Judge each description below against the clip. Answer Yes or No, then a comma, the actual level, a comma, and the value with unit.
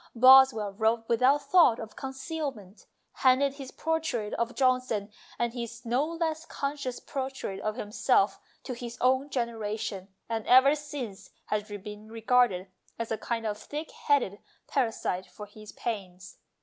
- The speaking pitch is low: No, high, 235 Hz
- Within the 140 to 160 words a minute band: Yes, average, 145 wpm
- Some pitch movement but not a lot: Yes, average, 4.0 semitones